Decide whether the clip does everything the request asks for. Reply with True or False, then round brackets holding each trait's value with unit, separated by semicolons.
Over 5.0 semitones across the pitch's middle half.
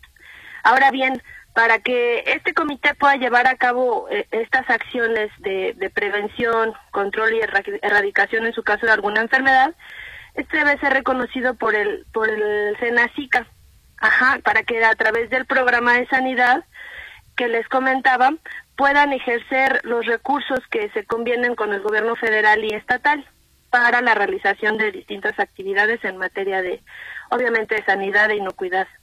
False (3.7 semitones)